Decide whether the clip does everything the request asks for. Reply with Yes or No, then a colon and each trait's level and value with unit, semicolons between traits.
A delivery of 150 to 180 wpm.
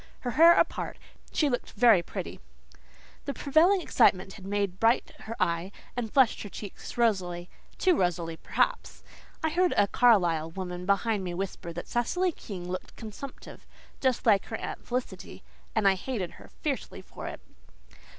Yes: average, 160 wpm